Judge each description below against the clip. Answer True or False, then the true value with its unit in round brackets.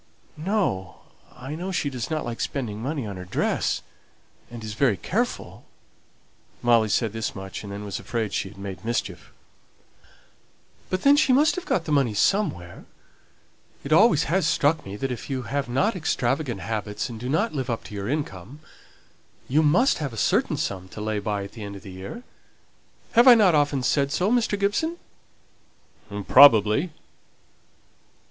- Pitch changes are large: True (7.3 semitones)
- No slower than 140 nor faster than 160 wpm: False (170 wpm)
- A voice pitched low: True (125 Hz)